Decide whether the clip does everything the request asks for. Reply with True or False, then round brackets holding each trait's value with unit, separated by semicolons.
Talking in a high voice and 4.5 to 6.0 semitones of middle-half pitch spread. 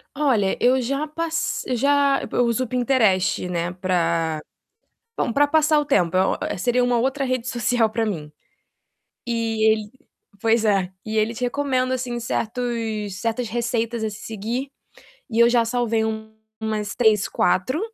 False (230 Hz; 3.0 semitones)